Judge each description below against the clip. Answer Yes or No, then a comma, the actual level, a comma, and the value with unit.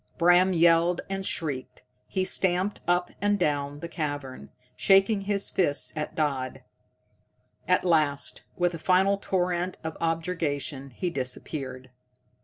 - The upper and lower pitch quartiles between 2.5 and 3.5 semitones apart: No, average, 4.2 semitones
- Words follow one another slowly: Yes, slow, 125 wpm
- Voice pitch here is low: No, medium, 170 Hz